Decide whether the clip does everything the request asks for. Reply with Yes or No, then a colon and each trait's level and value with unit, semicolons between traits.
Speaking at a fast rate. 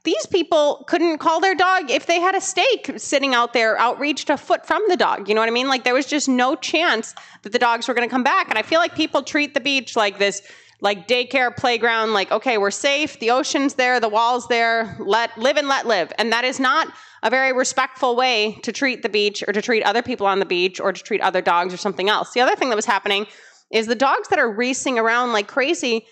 Yes: fast, 255 wpm